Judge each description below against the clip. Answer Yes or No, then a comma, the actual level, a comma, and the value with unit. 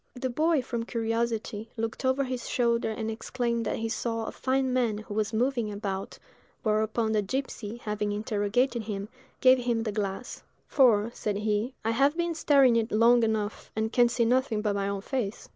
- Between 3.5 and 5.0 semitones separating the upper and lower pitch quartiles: No, average, 2.8 semitones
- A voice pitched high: Yes, high, 230 Hz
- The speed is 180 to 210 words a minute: Yes, average, 190 wpm